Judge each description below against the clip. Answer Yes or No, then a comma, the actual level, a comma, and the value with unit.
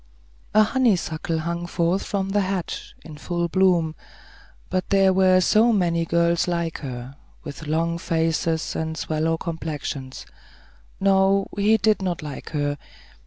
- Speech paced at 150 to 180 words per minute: No, slow, 135 wpm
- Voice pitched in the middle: Yes, medium, 170 Hz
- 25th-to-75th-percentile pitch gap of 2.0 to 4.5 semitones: Yes, average, 3.1 semitones